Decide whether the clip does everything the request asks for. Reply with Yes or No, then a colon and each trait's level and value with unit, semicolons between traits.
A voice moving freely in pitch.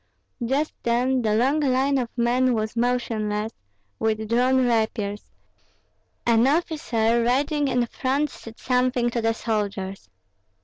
No: narrow, 2.6 semitones